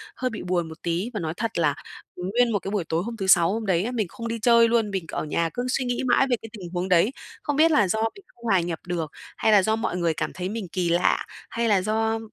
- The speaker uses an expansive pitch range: No, average, 4.7 semitones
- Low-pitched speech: No, high, 205 Hz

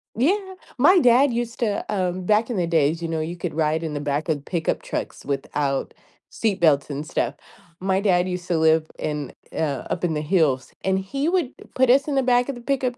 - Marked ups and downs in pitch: Yes, wide, 7.6 semitones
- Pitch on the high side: No, medium, 180 Hz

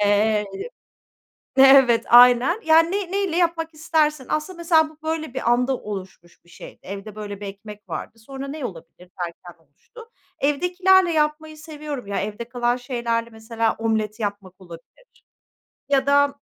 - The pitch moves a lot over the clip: Yes, wide, 6.9 semitones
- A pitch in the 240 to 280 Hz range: Yes, very high, 250 Hz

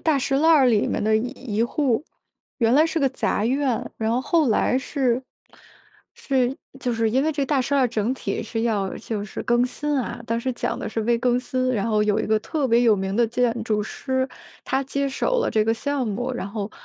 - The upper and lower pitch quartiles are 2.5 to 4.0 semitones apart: Yes, average, 3.4 semitones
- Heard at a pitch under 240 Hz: No, high, 245 Hz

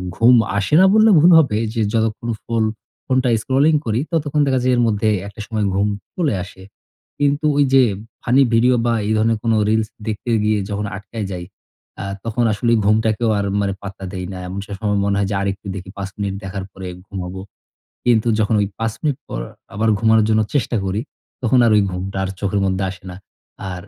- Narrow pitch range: No, average, 3.6 semitones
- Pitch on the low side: Yes, low, 110 Hz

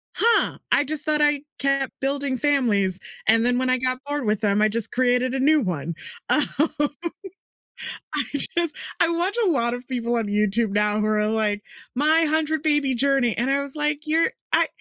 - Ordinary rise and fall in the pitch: Yes, average, 4.9 semitones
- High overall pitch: Yes, very high, 265 Hz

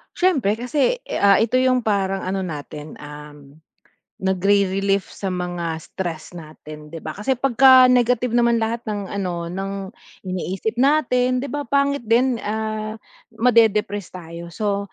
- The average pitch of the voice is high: Yes, high, 205 Hz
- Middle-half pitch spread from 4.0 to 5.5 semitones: Yes, average, 5.2 semitones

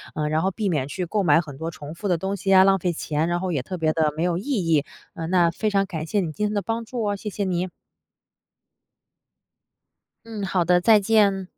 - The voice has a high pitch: No, medium, 180 Hz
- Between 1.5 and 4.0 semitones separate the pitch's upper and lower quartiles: Yes, average, 3.6 semitones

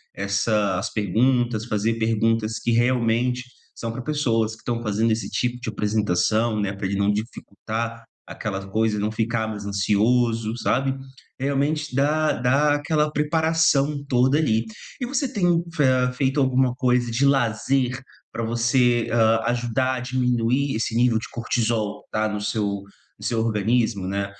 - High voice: No, low, 115 Hz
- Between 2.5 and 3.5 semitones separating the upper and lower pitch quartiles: Yes, average, 3.0 semitones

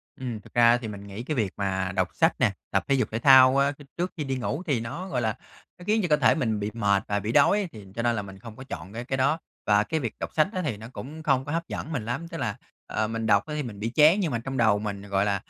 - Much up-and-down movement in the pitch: Yes, wide, 5.9 semitones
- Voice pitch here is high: No, low, 120 Hz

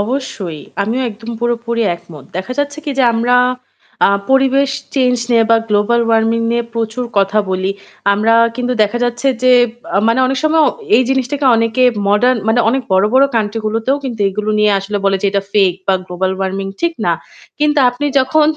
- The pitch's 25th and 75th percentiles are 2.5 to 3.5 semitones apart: No, average, 3.9 semitones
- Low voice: No, high, 230 Hz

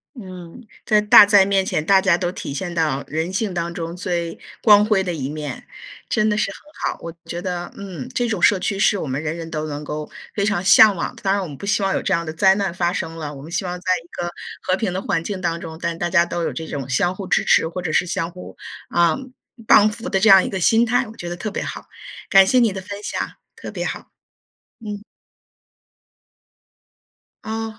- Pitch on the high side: No, medium, 180 Hz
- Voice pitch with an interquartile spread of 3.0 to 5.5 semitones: Yes, average, 3.4 semitones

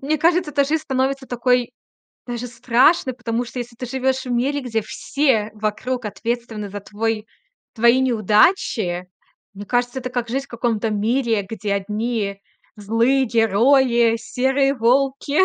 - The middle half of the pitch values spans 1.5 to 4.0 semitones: Yes, average, 3.1 semitones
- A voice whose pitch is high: Yes, high, 240 Hz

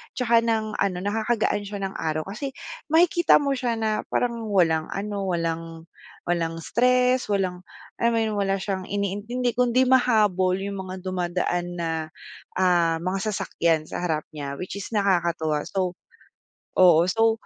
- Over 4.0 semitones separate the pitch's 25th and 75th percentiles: Yes, average, 4.5 semitones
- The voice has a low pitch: No, high, 195 Hz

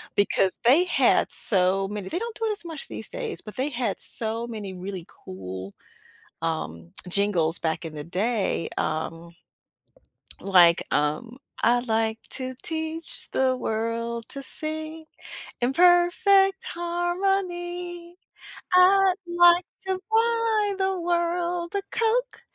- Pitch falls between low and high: No, very high, 270 Hz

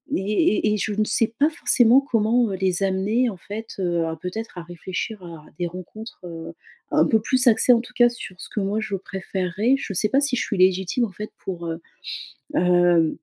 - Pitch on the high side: Yes, high, 200 Hz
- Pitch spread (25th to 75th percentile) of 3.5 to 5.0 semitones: Yes, average, 4.2 semitones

